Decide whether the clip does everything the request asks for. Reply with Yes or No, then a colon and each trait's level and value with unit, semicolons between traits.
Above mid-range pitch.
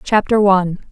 Yes: high, 195 Hz